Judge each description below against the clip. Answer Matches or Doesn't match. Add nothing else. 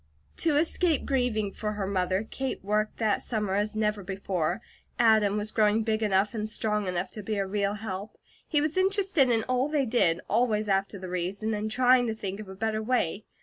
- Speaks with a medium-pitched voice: Doesn't match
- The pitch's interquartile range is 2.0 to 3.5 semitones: Matches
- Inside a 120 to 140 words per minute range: Doesn't match